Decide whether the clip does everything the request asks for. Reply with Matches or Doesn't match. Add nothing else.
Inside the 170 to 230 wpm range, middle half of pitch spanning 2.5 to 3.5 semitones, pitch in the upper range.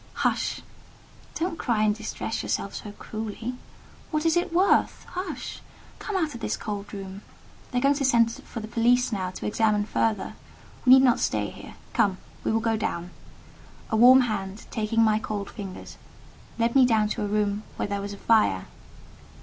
Matches